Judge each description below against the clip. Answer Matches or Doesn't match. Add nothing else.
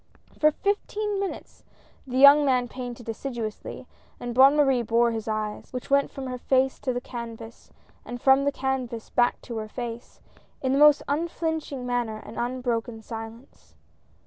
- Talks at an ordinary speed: Matches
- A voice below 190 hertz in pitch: Doesn't match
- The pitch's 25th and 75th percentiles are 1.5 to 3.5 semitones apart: Matches